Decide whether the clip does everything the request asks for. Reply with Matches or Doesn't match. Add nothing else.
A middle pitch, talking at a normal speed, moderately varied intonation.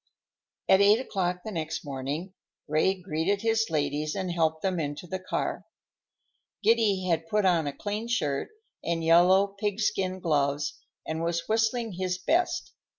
Matches